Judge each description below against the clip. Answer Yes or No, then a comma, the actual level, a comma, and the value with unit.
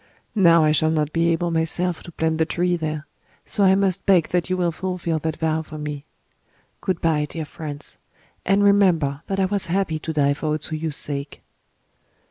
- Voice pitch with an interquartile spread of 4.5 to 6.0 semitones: No, average, 2.8 semitones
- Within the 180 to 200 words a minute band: Yes, average, 195 wpm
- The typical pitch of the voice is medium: Yes, medium, 160 Hz